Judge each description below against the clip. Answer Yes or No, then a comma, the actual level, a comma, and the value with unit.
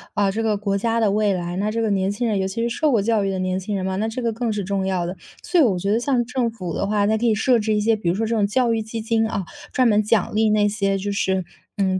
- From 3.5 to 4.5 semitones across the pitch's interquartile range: No, narrow, 2.6 semitones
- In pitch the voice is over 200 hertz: Yes, high, 210 Hz